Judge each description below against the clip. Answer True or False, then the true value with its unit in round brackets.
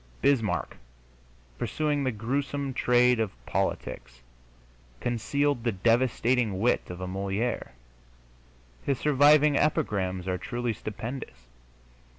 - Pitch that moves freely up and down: True (5.9 semitones)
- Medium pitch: False (120 Hz)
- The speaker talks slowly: True (100 wpm)